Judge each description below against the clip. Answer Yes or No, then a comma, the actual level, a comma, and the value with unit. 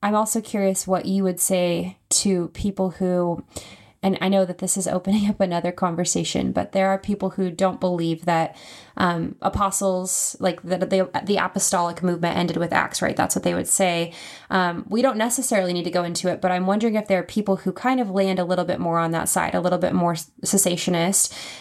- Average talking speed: No, fast, 215 wpm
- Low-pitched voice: No, medium, 185 Hz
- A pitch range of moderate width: No, narrow, 1.8 semitones